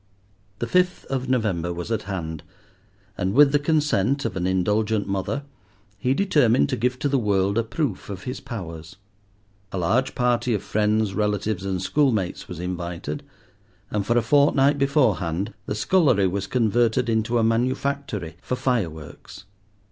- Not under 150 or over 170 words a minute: Yes, average, 155 wpm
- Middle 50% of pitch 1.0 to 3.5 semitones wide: No, average, 5.2 semitones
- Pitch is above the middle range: No, low, 110 Hz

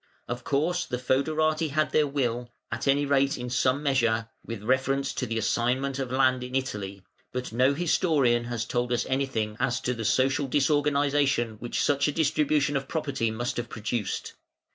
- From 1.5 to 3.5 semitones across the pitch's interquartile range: Yes, average, 2.8 semitones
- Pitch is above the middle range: No, low, 130 Hz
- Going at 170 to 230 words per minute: Yes, average, 175 wpm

